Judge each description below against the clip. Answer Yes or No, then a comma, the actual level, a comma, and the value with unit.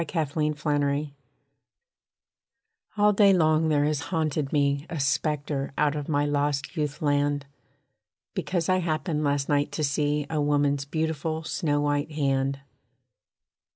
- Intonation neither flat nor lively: No, narrow, 1.6 semitones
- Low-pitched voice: No, medium, 145 Hz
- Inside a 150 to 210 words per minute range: No, slow, 135 wpm